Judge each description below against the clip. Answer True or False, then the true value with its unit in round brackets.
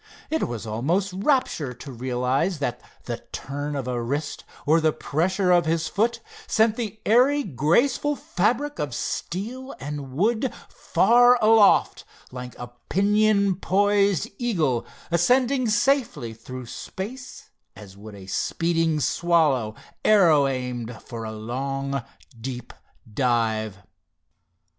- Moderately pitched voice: True (160 Hz)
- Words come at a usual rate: False (120 wpm)